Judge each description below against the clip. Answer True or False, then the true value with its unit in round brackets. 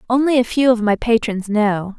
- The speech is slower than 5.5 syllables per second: True (5.1 syllables/s)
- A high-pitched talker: True (225 Hz)